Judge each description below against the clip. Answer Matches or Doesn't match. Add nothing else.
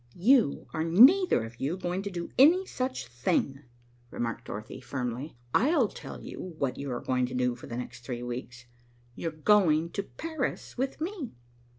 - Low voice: Doesn't match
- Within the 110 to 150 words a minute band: Doesn't match